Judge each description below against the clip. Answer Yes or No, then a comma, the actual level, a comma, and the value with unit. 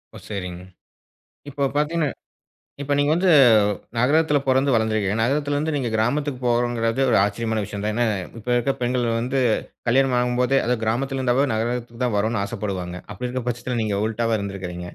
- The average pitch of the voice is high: No, low, 120 Hz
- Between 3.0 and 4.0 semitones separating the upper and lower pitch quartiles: Yes, average, 3.6 semitones